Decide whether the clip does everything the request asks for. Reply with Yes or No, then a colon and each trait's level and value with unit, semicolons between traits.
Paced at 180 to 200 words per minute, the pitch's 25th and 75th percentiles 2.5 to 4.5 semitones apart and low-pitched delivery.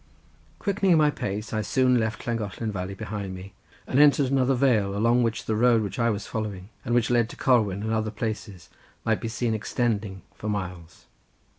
Yes: average, 185 wpm; average, 3.2 semitones; low, 110 Hz